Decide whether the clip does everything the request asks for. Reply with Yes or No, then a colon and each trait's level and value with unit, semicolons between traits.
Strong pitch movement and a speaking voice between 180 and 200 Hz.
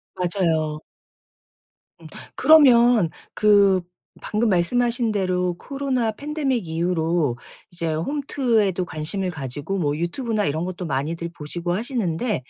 Yes: wide, 6.1 semitones; medium, 185 Hz